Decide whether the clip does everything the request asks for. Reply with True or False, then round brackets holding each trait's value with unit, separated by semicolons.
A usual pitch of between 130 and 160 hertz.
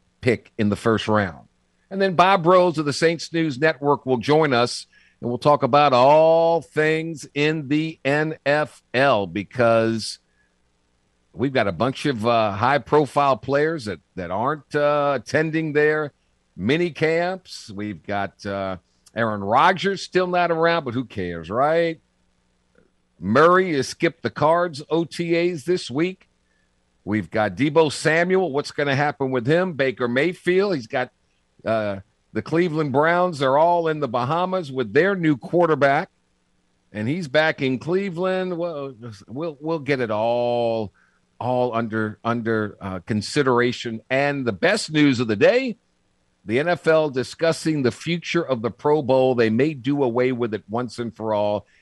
True (135 Hz)